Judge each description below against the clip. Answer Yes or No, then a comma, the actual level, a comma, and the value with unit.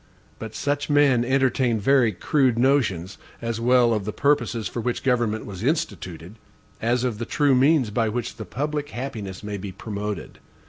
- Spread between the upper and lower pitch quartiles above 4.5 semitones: No, average, 4.2 semitones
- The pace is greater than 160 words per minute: Yes, average, 170 wpm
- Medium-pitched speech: No, low, 120 Hz